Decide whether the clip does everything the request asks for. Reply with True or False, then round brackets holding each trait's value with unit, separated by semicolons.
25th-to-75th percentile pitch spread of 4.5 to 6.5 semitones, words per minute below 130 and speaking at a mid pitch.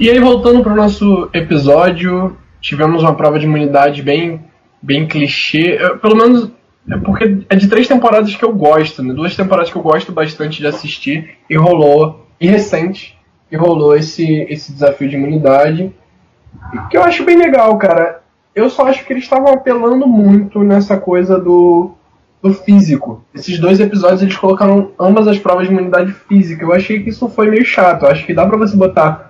False (5.1 semitones; 185 wpm; 180 Hz)